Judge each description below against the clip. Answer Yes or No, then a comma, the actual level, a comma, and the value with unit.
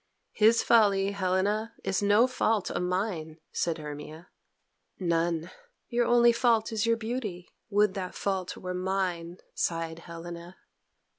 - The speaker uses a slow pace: Yes, slow, 130 wpm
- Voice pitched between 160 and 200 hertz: Yes, high, 190 Hz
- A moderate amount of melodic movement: Yes, average, 4.2 semitones